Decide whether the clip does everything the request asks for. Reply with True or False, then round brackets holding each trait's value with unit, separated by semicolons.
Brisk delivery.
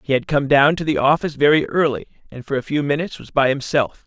True (250 wpm)